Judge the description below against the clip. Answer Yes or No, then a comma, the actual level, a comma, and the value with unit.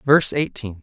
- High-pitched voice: No, low, 120 Hz